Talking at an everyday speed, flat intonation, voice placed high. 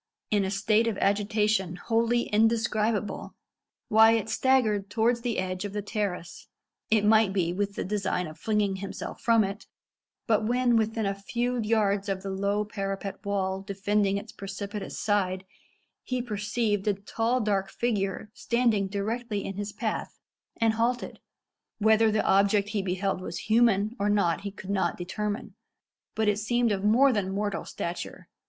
Yes: average, 160 wpm; narrow, 2.1 semitones; high, 210 Hz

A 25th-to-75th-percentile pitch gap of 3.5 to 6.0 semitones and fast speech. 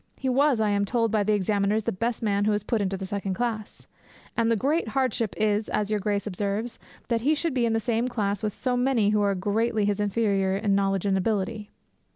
No: narrow, 2.5 semitones; fast, 230 wpm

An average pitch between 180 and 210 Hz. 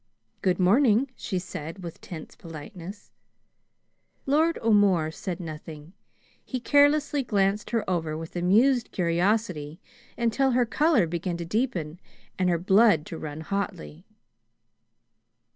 Yes: high, 190 Hz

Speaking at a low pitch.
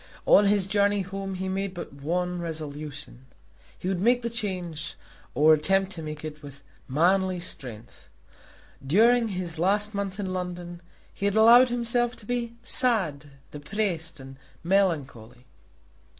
No: medium, 185 Hz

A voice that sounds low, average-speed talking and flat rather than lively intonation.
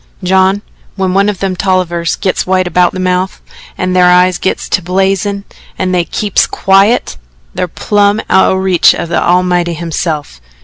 No: medium, 185 Hz; average, 170 wpm; narrow, 1.4 semitones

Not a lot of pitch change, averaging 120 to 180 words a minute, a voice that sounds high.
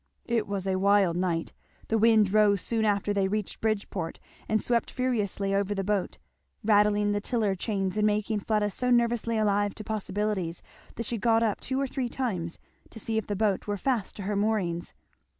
No: narrow, 2.1 semitones; average, 190 wpm; high, 210 Hz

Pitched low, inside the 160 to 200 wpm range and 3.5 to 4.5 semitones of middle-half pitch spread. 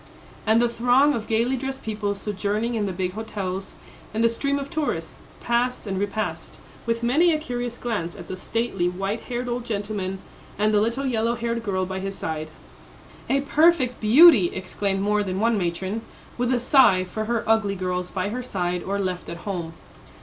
No: high, 215 Hz; average, 185 wpm; average, 4.1 semitones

